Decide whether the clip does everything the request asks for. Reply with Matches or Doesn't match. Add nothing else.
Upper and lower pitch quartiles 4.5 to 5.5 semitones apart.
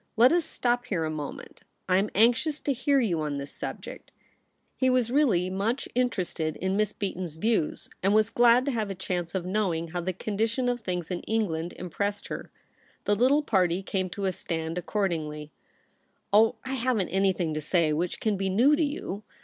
Matches